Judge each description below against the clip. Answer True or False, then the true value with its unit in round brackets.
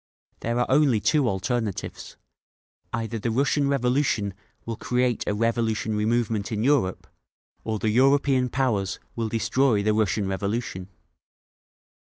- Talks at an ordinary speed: False (125 wpm)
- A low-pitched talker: True (115 Hz)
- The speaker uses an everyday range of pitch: True (3.2 semitones)